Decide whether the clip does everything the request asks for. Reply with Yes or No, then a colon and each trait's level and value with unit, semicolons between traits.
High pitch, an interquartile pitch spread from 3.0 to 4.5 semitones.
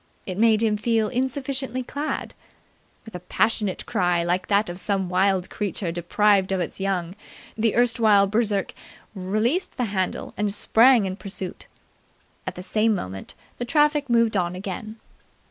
Yes: high, 210 Hz; average, 3.7 semitones